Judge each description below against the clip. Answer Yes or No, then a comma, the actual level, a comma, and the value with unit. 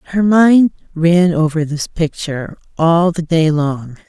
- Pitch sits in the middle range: Yes, medium, 165 Hz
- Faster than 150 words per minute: No, average, 145 wpm